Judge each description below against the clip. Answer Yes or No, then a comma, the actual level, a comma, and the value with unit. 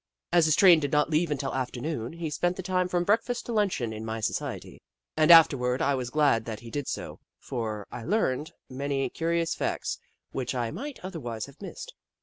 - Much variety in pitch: Yes, wide, 5.8 semitones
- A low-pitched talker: No, medium, 145 Hz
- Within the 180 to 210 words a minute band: Yes, average, 195 wpm